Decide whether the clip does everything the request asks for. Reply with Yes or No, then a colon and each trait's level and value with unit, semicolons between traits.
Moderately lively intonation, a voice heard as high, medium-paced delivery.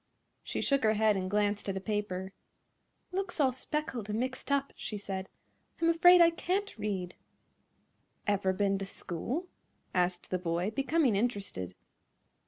No: wide, 6.6 semitones; high, 210 Hz; average, 155 wpm